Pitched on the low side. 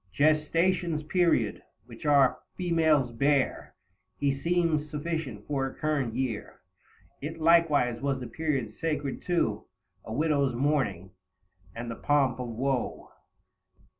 No: medium, 145 Hz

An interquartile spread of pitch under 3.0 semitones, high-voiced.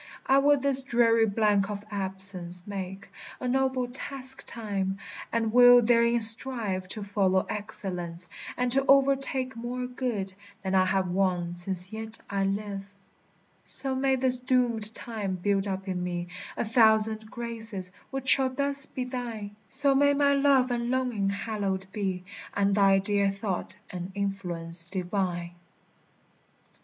No: average, 4.7 semitones; high, 215 Hz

